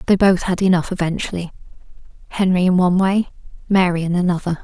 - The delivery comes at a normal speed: Yes, average, 155 wpm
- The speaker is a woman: Yes, female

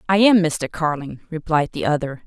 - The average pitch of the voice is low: No, medium, 165 Hz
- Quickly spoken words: No, average, 185 wpm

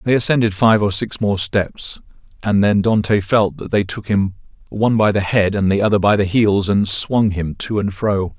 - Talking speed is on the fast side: Yes, fast, 220 wpm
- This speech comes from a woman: No, male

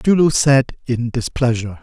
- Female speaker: No, male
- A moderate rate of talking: Yes, average, 165 wpm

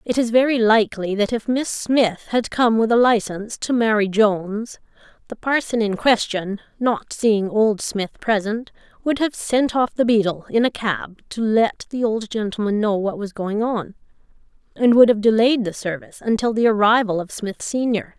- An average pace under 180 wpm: No, average, 185 wpm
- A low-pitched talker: No, high, 220 Hz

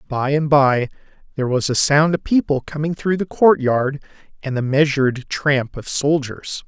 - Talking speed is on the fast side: No, average, 170 wpm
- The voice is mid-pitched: Yes, medium, 145 Hz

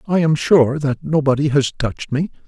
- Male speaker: Yes, male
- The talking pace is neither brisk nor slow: Yes, average, 195 wpm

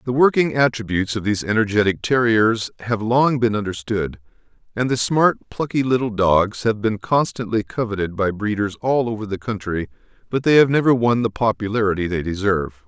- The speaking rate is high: No, average, 170 wpm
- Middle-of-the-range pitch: No, low, 110 Hz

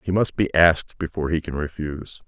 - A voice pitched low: Yes, very low, 80 Hz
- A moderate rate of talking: No, fast, 210 wpm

